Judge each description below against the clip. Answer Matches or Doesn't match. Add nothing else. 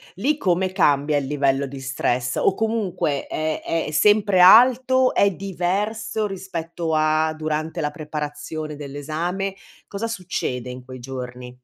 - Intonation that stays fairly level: Doesn't match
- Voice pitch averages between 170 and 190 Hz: Doesn't match